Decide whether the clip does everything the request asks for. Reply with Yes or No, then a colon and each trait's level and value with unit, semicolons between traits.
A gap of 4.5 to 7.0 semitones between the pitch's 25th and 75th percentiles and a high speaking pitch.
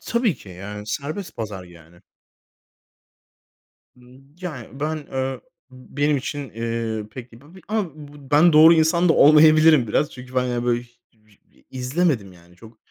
No: wide, 5.4 semitones; low, 130 Hz